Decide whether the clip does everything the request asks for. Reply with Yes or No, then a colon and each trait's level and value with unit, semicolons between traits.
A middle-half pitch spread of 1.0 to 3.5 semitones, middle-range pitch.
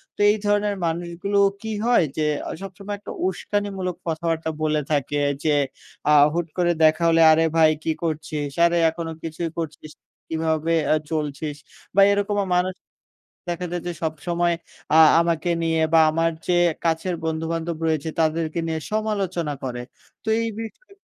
Yes: average, 2.7 semitones; medium, 165 Hz